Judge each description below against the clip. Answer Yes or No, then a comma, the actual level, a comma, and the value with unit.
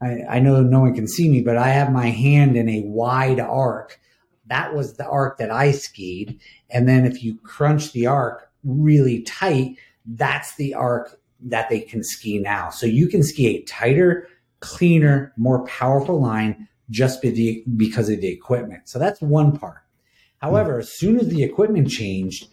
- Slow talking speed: No, average, 175 wpm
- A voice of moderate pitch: No, low, 130 Hz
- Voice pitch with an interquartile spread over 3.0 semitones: Yes, average, 3.7 semitones